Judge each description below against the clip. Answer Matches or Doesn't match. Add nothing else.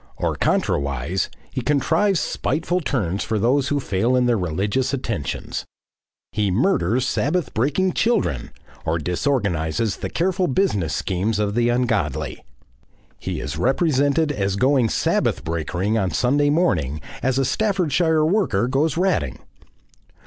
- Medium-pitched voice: Doesn't match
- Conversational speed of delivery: Doesn't match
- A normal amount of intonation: Doesn't match